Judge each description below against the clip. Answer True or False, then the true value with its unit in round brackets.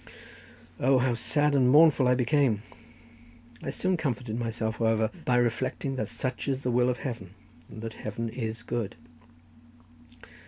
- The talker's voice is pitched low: True (120 Hz)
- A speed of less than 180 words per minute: True (150 wpm)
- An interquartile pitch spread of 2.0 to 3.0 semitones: True (2.7 semitones)